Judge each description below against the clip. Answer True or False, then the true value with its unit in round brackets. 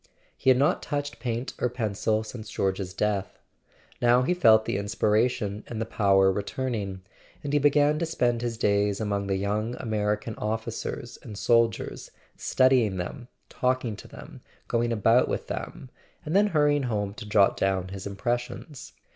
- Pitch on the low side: True (115 Hz)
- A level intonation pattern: False (3.8 semitones)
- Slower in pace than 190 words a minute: True (165 wpm)